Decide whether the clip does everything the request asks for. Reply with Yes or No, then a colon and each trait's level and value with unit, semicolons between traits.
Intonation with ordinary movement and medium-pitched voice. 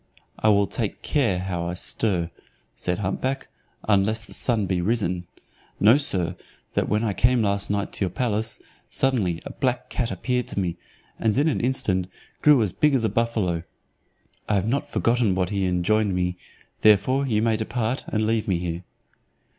No: average, 4.2 semitones; low, 105 Hz